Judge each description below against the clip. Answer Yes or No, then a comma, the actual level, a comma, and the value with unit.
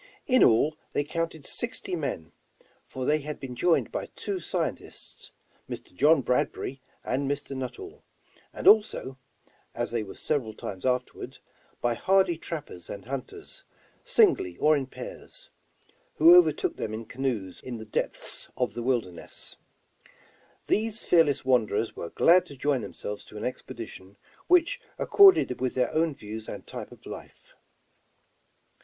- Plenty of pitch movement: Yes, wide, 8.1 semitones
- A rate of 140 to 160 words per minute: Yes, average, 150 wpm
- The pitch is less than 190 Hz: Yes, low, 135 Hz